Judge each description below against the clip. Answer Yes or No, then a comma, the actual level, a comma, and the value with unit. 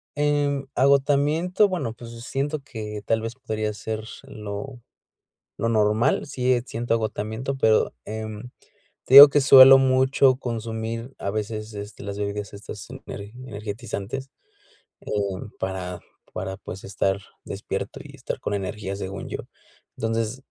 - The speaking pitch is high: No, low, 115 Hz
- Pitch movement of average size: Yes, average, 4.3 semitones